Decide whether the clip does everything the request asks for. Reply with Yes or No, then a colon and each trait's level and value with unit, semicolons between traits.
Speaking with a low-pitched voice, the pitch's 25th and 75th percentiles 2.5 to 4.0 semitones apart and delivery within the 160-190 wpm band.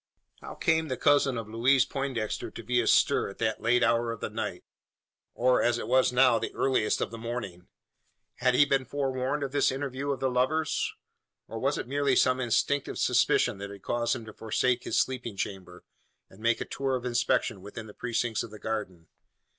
No: low, 125 Hz; average, 3.0 semitones; average, 200 wpm